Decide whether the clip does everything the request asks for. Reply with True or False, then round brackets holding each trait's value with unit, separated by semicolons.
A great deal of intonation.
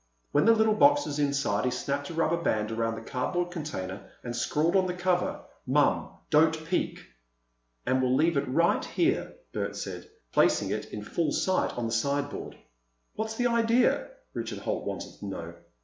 True (6.4 semitones)